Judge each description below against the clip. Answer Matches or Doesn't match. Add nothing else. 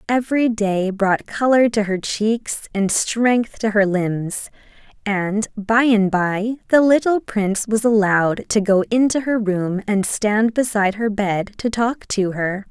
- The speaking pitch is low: Doesn't match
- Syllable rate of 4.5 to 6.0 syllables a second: Doesn't match